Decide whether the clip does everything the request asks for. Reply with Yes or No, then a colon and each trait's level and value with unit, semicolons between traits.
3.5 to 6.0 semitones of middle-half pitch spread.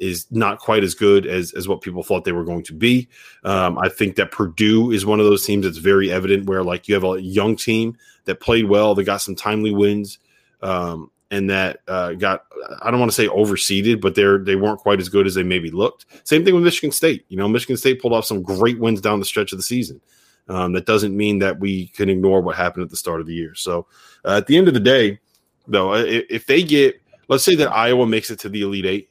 No: average, 2.8 semitones